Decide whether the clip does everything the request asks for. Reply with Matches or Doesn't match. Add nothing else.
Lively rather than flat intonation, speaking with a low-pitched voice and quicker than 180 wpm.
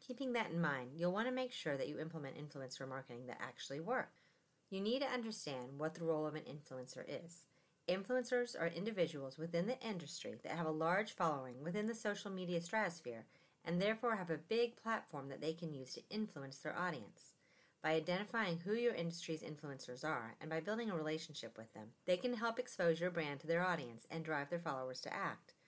Doesn't match